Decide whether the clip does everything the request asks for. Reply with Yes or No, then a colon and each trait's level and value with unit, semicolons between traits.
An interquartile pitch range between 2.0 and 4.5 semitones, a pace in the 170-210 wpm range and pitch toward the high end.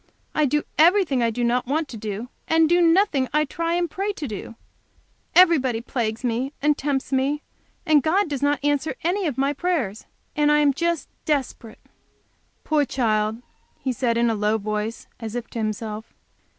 No: average, 5.2 semitones; average, 180 wpm; very high, 275 Hz